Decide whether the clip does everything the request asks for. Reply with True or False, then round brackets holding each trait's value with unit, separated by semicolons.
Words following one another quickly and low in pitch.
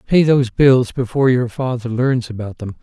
False (190 wpm; 125 Hz)